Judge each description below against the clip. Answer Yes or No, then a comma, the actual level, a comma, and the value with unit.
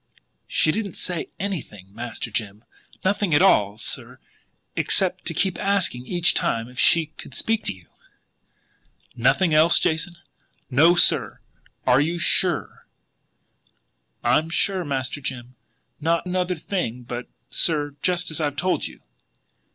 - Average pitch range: No, wide, 6.2 semitones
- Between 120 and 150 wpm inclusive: Yes, slow, 135 wpm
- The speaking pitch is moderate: Yes, medium, 155 Hz